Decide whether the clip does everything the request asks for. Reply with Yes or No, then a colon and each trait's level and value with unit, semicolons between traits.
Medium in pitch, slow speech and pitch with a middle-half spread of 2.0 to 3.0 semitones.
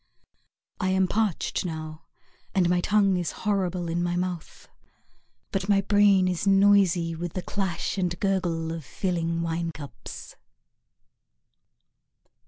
Yes: medium, 180 Hz; slow, 125 wpm; narrow, 2.6 semitones